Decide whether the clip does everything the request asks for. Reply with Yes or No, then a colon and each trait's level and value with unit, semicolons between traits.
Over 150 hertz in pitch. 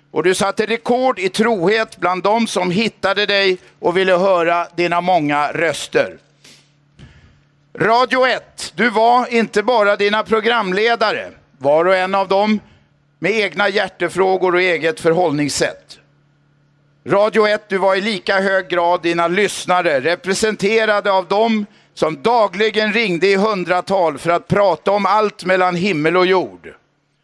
Yes: high, 190 Hz